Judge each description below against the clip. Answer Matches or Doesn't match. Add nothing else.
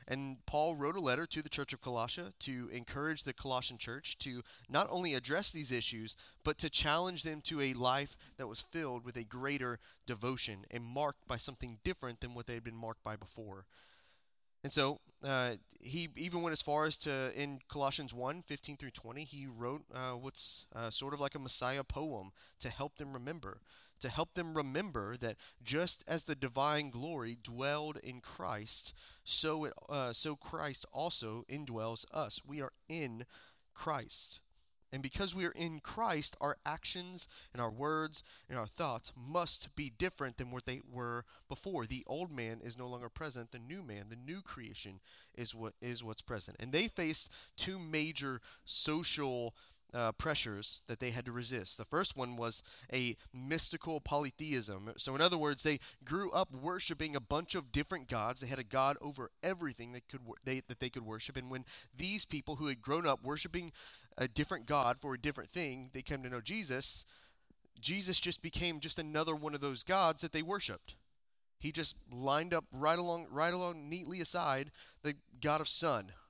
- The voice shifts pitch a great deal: Doesn't match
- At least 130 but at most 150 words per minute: Doesn't match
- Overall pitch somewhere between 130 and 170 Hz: Matches